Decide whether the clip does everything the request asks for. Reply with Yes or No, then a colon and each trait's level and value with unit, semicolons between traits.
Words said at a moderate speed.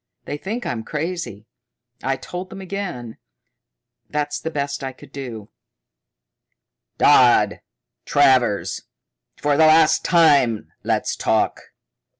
No: slow, 110 wpm